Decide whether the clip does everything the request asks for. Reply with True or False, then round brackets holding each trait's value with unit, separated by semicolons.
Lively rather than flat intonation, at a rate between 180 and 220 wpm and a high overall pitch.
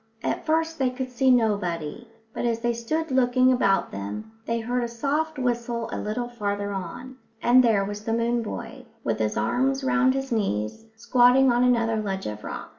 False (3.5 semitones; 190 wpm; 235 Hz)